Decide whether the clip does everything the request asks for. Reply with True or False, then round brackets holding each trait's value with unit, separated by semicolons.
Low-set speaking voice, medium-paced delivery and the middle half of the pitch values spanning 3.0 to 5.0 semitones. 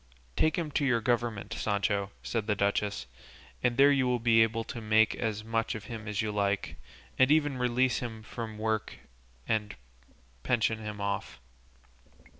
False (110 Hz; 165 wpm; 2.6 semitones)